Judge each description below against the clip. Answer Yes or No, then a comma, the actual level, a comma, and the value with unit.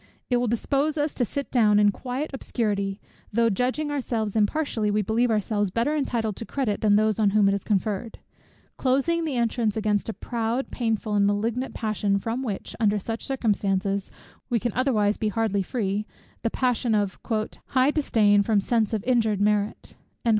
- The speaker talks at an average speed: Yes, average, 175 wpm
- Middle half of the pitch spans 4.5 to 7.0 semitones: No, average, 3.3 semitones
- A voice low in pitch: No, high, 220 Hz